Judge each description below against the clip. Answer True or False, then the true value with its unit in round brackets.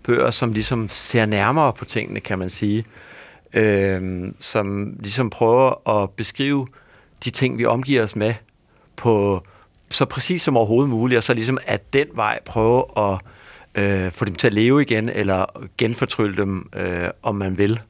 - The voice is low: True (110 Hz)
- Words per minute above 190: False (170 wpm)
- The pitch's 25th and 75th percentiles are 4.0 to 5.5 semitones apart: False (3.6 semitones)